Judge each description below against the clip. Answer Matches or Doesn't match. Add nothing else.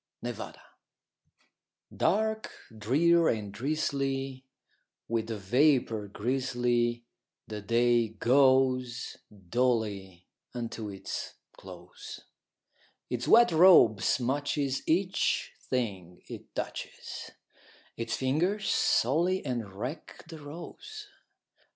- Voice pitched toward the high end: Doesn't match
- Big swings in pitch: Doesn't match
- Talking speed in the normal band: Doesn't match